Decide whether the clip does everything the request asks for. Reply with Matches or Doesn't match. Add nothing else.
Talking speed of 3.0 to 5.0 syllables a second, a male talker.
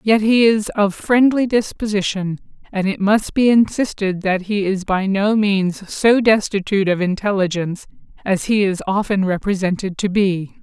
Doesn't match